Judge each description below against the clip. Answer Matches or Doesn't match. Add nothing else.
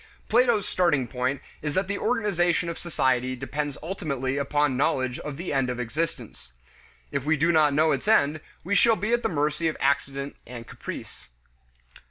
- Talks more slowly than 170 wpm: Doesn't match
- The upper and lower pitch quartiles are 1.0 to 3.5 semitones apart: Doesn't match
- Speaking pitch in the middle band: Matches